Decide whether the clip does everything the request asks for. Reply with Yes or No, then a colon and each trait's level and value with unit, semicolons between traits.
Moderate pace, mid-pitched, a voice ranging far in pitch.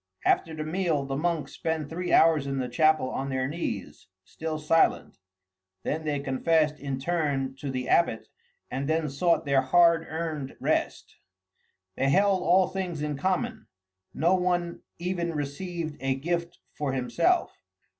No: average, 150 wpm; medium, 155 Hz; average, 3.9 semitones